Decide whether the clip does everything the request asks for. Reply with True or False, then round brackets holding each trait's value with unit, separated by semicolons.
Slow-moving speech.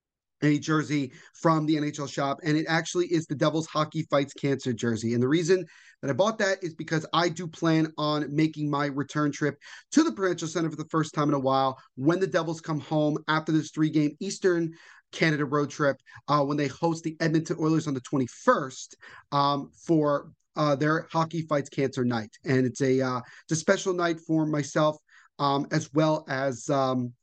False (195 wpm)